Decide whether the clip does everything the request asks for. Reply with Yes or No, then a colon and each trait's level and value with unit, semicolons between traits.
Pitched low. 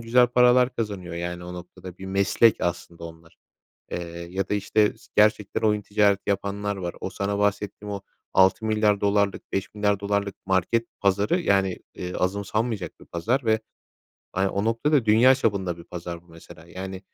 Yes: low, 100 Hz